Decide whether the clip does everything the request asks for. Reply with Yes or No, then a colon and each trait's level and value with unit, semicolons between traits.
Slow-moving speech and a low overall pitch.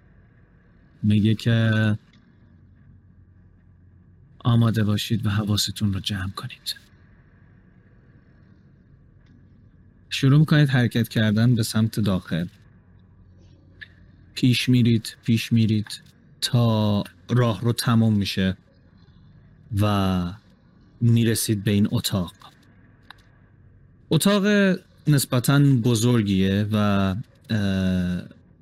Yes: slow, 70 wpm; low, 110 Hz